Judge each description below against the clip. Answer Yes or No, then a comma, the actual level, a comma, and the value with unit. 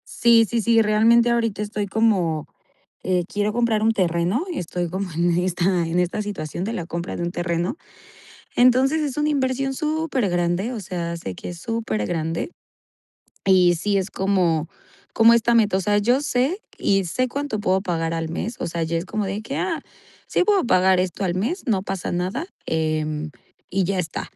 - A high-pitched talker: Yes, high, 195 Hz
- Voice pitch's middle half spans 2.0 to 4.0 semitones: No, average, 5.2 semitones